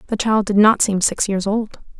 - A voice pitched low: No, high, 205 Hz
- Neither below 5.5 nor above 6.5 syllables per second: No, 5.0 syllables/s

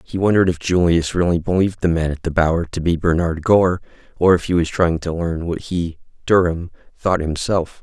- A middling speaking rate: Yes, average, 190 wpm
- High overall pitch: No, very low, 85 Hz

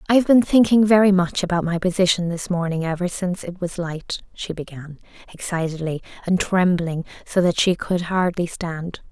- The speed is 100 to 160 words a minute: No, average, 170 wpm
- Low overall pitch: No, medium, 180 Hz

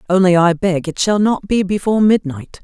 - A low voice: No, high, 190 Hz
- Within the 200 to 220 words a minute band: Yes, fast, 205 wpm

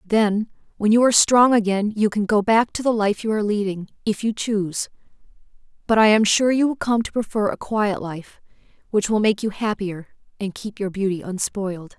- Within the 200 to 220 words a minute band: Yes, fast, 205 wpm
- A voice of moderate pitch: No, high, 210 Hz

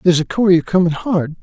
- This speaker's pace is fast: No, average, 170 wpm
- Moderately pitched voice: Yes, medium, 175 Hz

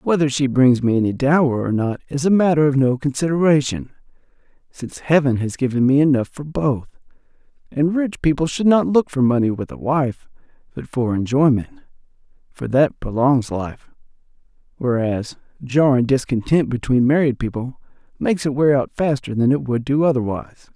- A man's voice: Yes, male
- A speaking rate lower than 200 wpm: Yes, average, 160 wpm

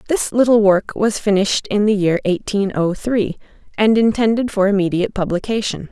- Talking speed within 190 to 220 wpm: No, average, 160 wpm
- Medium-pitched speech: No, high, 205 Hz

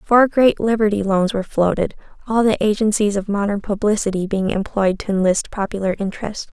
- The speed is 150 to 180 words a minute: Yes, average, 165 wpm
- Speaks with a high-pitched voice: Yes, high, 205 Hz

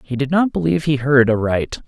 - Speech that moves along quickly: Yes, fast, 225 wpm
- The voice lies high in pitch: No, low, 135 Hz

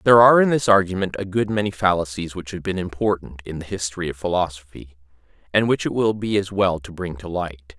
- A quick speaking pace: Yes, fast, 225 wpm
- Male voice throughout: Yes, male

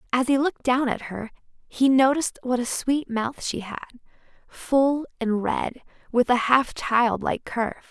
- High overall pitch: Yes, very high, 250 Hz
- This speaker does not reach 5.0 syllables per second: Yes, 4.5 syllables/s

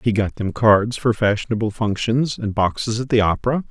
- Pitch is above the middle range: No, low, 110 Hz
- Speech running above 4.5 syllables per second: Yes, 5.3 syllables/s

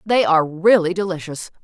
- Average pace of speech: Yes, average, 145 wpm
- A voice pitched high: No, medium, 175 Hz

